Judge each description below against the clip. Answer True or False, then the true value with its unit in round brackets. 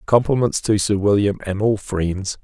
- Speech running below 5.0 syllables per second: True (4.5 syllables/s)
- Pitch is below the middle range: True (105 Hz)